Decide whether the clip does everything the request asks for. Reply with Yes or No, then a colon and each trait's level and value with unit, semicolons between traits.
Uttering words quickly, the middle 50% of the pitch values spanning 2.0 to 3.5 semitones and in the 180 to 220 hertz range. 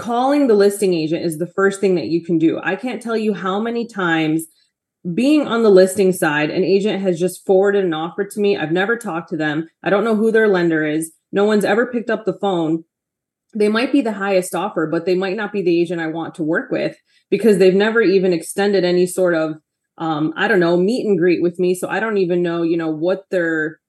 Yes: fast, 240 wpm; average, 3.2 semitones; medium, 185 Hz